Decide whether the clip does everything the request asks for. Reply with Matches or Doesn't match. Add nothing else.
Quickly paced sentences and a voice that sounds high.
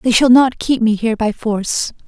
Matches